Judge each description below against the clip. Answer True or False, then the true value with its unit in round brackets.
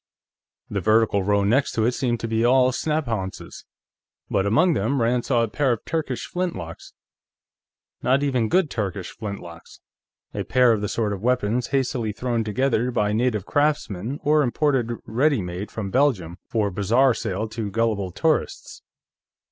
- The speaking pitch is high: False (115 Hz)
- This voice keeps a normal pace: True (155 wpm)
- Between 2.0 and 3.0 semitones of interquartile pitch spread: False (4.3 semitones)